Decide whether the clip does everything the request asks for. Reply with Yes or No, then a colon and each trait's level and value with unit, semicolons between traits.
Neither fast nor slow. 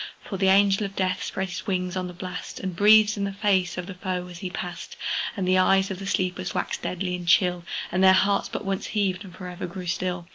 No: fast, 250 wpm